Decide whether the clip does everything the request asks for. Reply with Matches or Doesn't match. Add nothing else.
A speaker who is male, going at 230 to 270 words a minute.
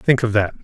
Doesn't match